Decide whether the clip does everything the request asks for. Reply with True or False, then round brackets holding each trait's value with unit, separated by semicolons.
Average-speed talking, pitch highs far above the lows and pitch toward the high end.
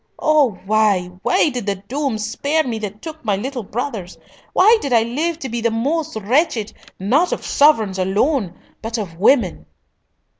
True (165 wpm; 6.0 semitones; 230 Hz)